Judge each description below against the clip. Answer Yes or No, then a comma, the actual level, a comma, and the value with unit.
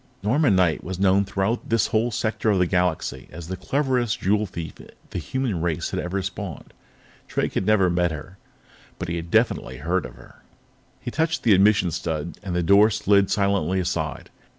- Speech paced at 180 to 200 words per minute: Yes, average, 185 wpm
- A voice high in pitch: No, very low, 95 Hz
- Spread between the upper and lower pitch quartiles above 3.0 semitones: Yes, average, 3.7 semitones